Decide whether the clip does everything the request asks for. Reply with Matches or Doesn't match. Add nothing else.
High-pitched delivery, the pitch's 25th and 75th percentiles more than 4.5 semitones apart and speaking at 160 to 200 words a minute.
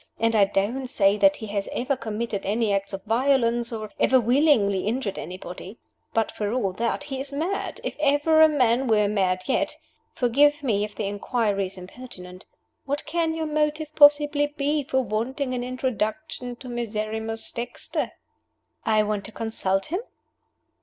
Matches